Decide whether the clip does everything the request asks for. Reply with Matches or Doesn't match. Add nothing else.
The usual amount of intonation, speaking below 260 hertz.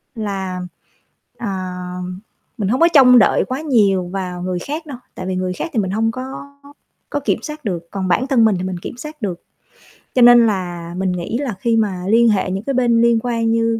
Matches